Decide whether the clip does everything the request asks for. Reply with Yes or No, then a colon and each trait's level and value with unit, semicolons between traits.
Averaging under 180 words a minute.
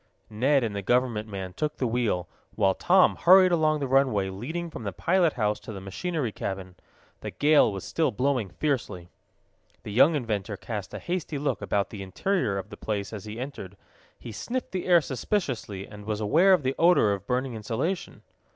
No: average, 190 wpm